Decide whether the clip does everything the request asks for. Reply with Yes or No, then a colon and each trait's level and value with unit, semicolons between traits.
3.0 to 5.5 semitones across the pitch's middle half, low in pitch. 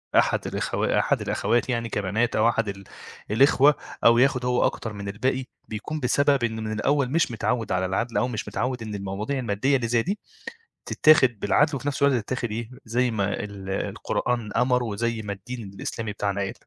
Yes: average, 3.5 semitones; low, 115 Hz